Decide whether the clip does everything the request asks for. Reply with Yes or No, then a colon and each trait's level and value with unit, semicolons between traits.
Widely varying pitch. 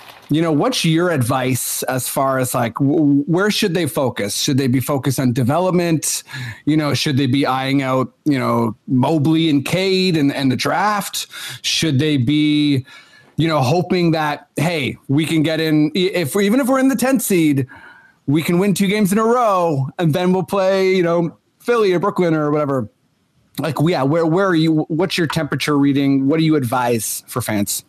No: average, 4.6 semitones